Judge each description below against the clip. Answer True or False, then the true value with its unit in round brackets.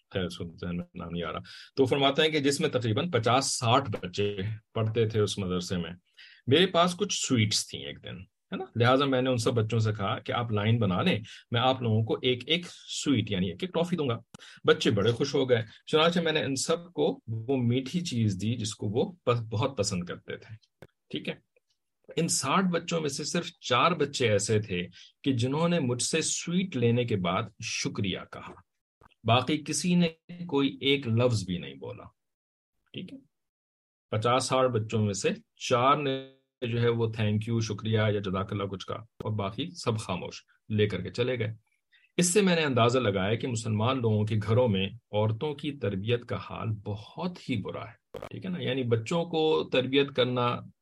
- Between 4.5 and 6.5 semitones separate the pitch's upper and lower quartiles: True (5.2 semitones)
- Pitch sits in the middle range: False (120 Hz)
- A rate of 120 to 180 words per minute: False (195 wpm)